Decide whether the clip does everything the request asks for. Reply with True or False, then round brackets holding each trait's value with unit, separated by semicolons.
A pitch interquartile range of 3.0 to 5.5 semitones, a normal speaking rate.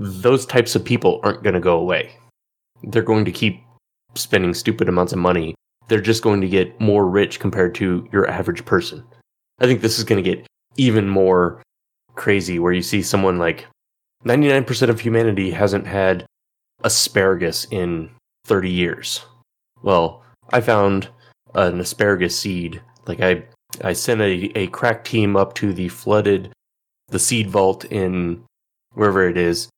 True (3.7 semitones; 155 wpm)